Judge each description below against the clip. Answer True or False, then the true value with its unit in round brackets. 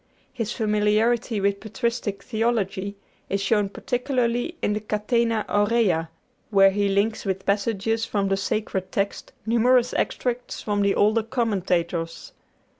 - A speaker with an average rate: False (125 wpm)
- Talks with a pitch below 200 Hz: False (210 Hz)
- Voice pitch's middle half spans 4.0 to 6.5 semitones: False (2.8 semitones)